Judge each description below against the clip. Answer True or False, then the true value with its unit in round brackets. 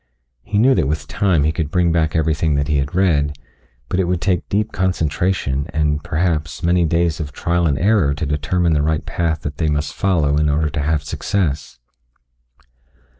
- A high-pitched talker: False (80 Hz)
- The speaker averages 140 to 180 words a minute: False (190 wpm)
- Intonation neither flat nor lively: True (3.0 semitones)